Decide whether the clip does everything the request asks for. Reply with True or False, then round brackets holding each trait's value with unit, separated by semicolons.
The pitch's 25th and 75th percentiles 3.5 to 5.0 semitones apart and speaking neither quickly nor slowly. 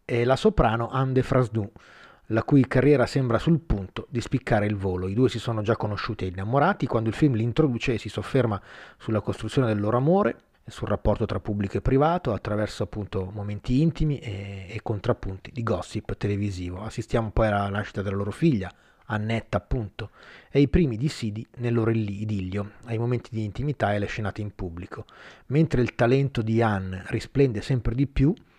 False (3.9 semitones; 185 wpm)